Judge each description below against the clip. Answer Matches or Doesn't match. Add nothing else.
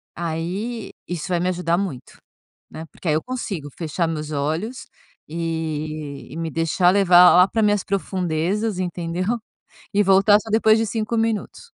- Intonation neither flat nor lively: Matches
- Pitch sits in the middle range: Matches